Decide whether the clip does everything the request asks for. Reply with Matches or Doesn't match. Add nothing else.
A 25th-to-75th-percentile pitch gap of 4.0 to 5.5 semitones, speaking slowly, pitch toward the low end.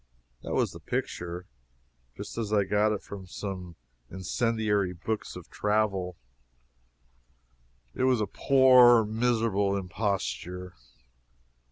Doesn't match